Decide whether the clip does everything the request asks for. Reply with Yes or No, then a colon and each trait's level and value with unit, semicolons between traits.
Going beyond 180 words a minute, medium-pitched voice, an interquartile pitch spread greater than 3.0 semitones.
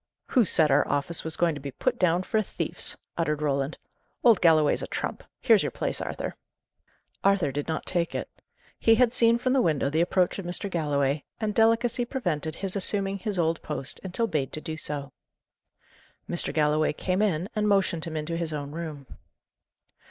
Yes: average, 190 wpm; medium, 170 Hz; average, 4.7 semitones